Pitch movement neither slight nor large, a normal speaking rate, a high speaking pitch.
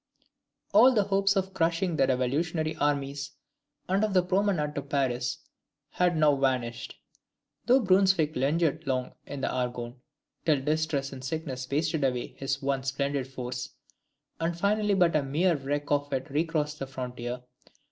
No: average, 4.2 semitones; average, 145 wpm; medium, 145 Hz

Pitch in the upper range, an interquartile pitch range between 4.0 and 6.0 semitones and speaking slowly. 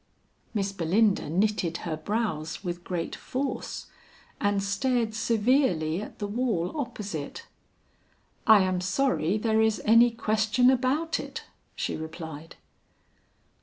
Yes: high, 210 Hz; average, 4.9 semitones; slow, 115 wpm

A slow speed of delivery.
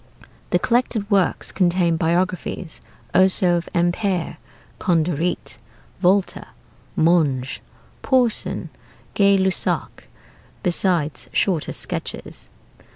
Yes: slow, 80 wpm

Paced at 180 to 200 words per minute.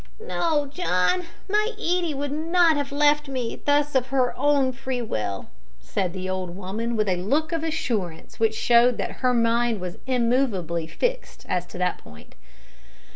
No: average, 165 wpm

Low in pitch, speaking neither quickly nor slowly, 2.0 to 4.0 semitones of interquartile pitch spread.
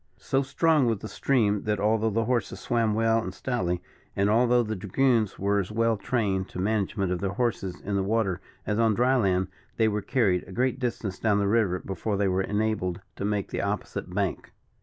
No: low, 105 Hz; fast, 210 wpm; average, 2.9 semitones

